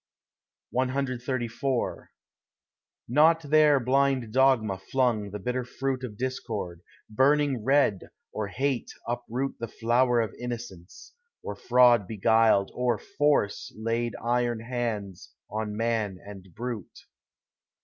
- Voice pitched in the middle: No, low, 120 Hz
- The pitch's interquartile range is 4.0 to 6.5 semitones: No, average, 3.3 semitones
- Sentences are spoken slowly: Yes, slow, 110 wpm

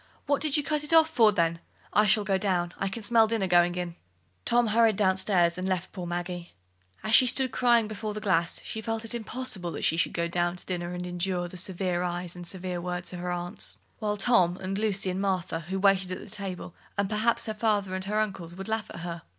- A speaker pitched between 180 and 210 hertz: Yes, high, 190 Hz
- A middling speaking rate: No, fast, 240 wpm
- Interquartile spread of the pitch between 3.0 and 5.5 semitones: Yes, average, 3.5 semitones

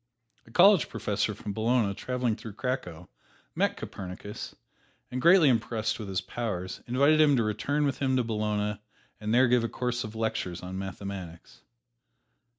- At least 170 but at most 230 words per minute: No, average, 155 wpm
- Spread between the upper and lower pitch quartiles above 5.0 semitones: No, average, 4.2 semitones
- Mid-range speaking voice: No, low, 110 Hz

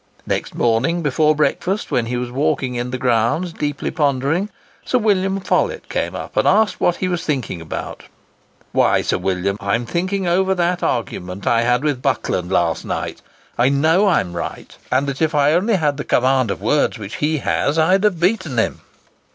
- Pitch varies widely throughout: Yes, wide, 6.3 semitones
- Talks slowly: No, average, 190 wpm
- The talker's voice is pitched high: No, medium, 145 Hz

